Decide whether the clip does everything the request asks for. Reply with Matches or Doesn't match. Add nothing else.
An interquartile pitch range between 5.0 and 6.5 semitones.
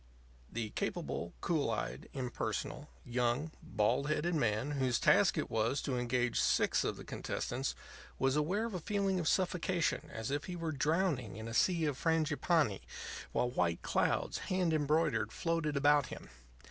Matches